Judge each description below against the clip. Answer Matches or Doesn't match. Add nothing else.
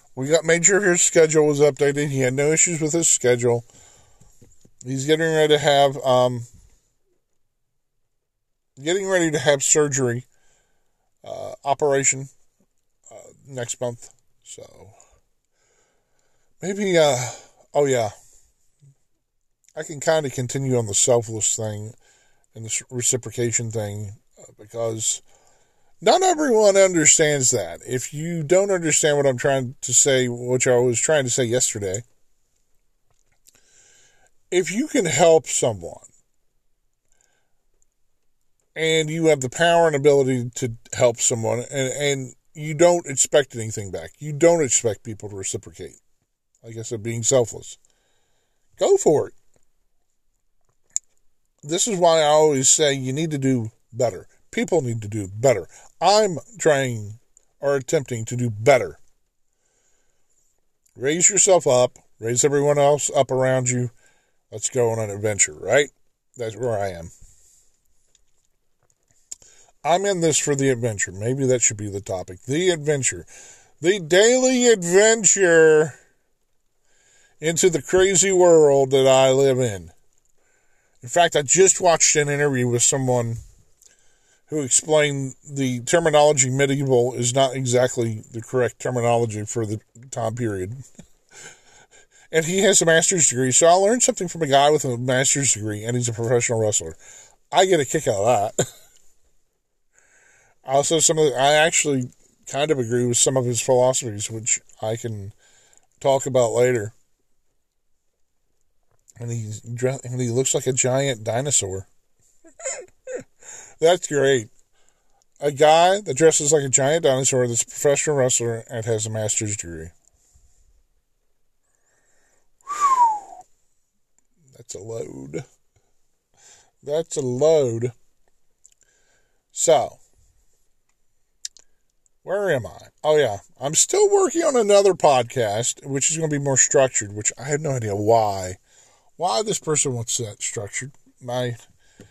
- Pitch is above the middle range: Doesn't match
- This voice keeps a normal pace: Doesn't match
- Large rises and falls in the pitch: Doesn't match